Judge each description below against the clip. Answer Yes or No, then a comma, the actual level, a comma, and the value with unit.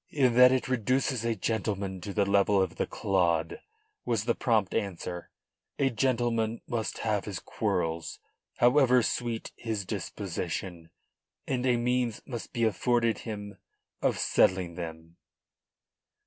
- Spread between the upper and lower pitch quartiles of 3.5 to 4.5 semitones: Yes, average, 4.2 semitones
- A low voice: Yes, low, 110 Hz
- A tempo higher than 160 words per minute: No, slow, 135 wpm